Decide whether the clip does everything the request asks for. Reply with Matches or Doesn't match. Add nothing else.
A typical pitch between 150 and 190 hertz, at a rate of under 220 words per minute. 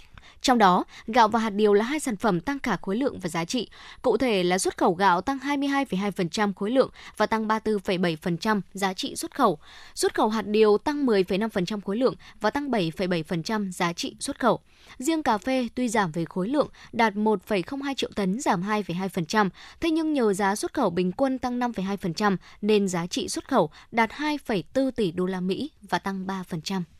Doesn't match